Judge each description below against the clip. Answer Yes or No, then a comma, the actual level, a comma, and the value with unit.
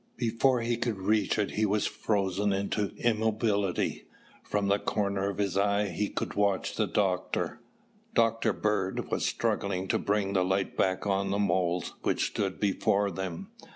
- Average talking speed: Yes, average, 160 wpm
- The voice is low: Yes, low, 100 Hz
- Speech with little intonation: Yes, narrow, 1.7 semitones